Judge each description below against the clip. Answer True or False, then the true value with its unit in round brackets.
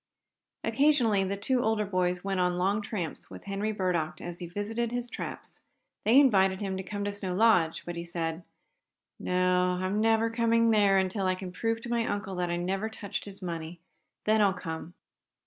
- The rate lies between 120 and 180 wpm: False (190 wpm)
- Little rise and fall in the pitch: False (3.3 semitones)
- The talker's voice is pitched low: False (195 Hz)